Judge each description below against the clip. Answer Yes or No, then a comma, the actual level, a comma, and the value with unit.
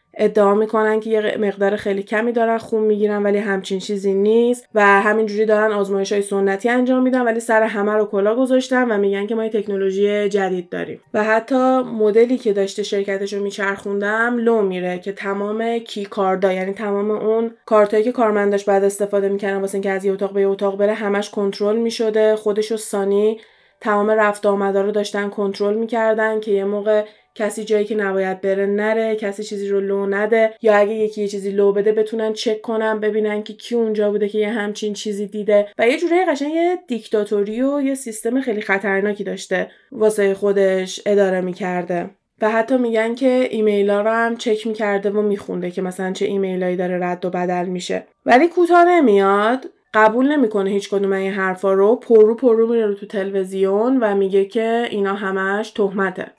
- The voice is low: No, high, 210 Hz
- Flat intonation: Yes, narrow, 1.9 semitones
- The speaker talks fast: Yes, fast, 185 wpm